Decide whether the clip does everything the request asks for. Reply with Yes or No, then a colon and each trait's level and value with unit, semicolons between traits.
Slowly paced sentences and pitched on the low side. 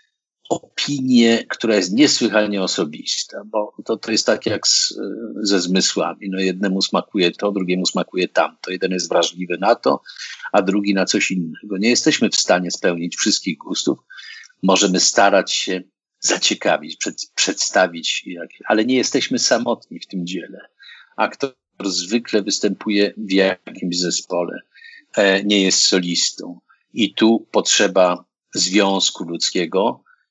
No: average, 130 wpm; very low, 95 Hz